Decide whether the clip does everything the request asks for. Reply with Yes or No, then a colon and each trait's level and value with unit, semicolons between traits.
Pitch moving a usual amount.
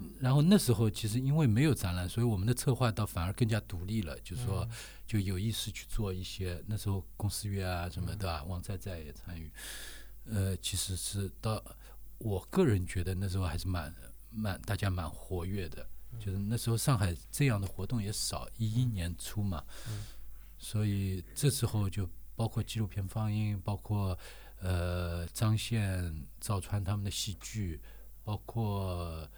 Yes: average, 3.5 semitones